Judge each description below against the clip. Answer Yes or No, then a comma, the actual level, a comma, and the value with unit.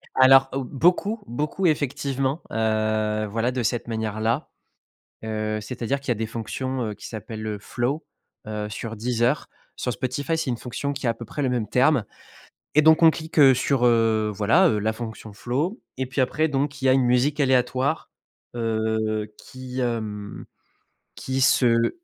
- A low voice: Yes, low, 125 Hz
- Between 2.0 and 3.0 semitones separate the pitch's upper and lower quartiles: No, average, 3.7 semitones